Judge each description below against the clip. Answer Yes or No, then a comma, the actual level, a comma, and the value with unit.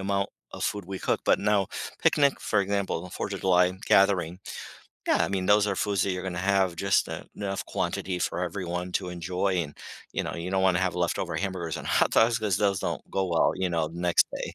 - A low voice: Yes, very low, 95 Hz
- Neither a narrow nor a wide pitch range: No, narrow, 1.9 semitones